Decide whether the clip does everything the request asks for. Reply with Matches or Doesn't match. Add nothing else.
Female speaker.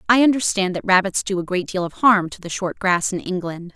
Matches